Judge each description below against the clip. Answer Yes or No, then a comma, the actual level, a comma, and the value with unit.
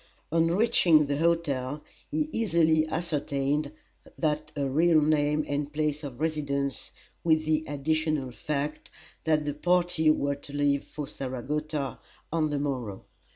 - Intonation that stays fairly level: Yes, narrow, 1.9 semitones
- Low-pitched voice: No, medium, 150 Hz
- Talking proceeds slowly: Yes, slow, 130 wpm